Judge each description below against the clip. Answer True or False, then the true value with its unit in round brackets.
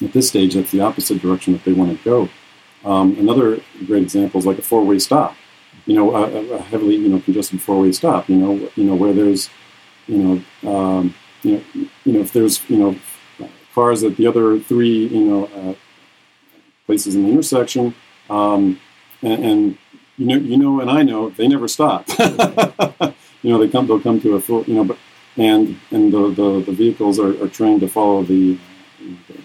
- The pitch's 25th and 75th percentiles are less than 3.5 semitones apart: False (4.9 semitones)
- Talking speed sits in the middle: True (175 wpm)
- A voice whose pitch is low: True (105 Hz)